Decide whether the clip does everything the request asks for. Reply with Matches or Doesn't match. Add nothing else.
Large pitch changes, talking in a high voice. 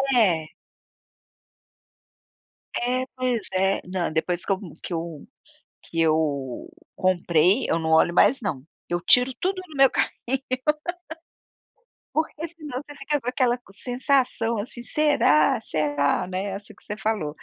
Matches